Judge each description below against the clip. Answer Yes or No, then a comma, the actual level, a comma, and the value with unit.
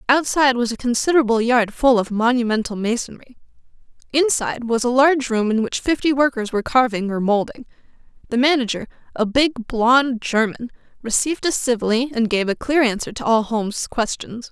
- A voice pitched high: Yes, high, 240 Hz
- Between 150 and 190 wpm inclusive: Yes, average, 165 wpm